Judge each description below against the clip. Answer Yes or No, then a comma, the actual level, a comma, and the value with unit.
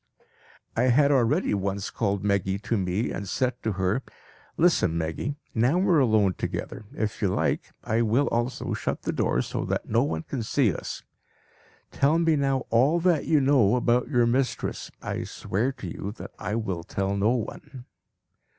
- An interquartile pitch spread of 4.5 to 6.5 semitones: Yes, average, 5.3 semitones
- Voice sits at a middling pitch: No, low, 115 Hz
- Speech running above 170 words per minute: Yes, average, 180 wpm